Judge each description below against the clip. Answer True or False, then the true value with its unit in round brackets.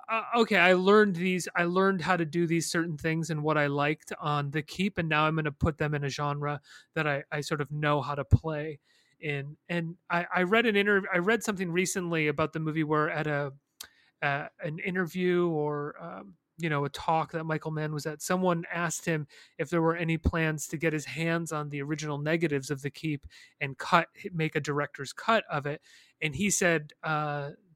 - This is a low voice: False (160 Hz)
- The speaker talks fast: True (220 wpm)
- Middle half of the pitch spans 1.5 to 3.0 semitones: True (2.7 semitones)